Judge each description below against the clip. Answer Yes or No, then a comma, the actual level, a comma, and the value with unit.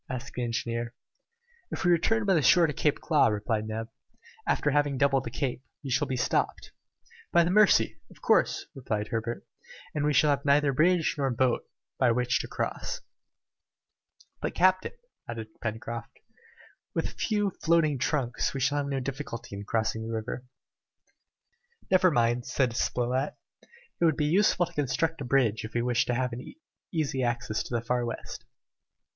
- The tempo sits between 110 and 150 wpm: No, average, 175 wpm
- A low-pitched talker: Yes, low, 130 Hz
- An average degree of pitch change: Yes, average, 4.2 semitones